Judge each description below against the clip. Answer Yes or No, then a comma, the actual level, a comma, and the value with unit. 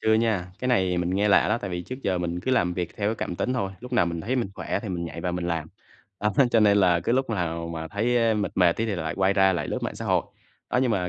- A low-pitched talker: Yes, very low, 95 Hz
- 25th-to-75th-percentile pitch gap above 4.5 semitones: No, average, 4.2 semitones